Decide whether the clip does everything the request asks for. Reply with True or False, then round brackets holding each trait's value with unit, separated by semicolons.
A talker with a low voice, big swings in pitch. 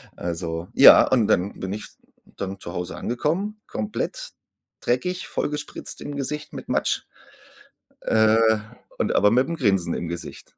True (110 Hz; 7.7 semitones)